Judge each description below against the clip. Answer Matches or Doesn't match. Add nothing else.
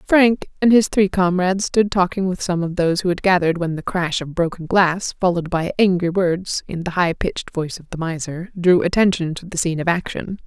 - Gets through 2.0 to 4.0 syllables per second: Doesn't match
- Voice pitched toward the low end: Doesn't match